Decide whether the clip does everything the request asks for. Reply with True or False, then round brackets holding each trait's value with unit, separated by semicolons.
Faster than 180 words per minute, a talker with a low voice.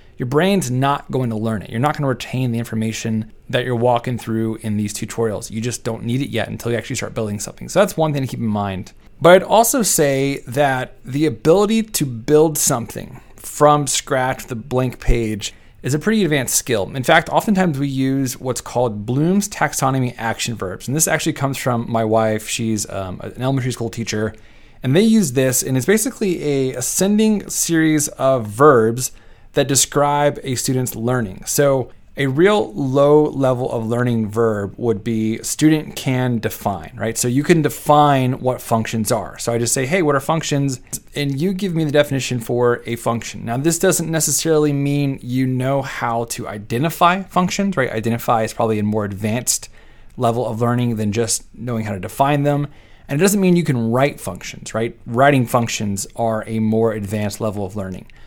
True (190 wpm; 125 Hz)